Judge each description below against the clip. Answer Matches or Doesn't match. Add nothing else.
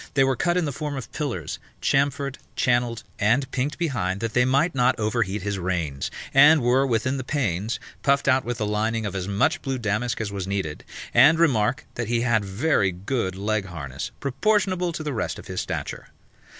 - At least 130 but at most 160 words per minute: Doesn't match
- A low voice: Matches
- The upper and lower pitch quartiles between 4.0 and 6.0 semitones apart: Matches